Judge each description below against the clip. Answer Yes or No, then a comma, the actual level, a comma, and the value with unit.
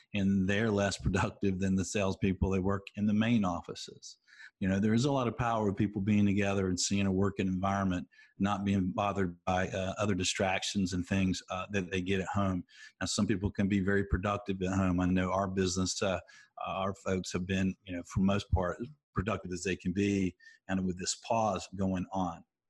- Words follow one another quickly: Yes, fast, 210 wpm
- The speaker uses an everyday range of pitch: No, narrow, 1.4 semitones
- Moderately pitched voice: No, very low, 95 Hz